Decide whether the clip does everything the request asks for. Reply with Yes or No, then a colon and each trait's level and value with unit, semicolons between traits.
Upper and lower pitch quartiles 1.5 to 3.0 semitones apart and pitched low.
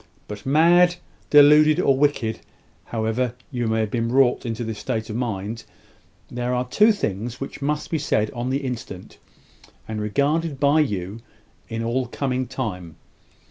No: average, 4.2 semitones; low, 125 Hz